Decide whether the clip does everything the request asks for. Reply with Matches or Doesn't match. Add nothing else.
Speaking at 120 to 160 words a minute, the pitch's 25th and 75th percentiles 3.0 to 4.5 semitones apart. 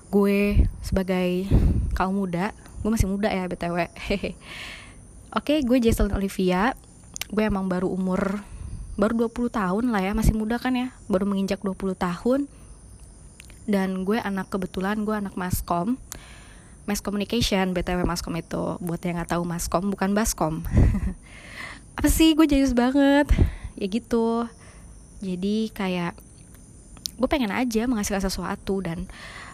Matches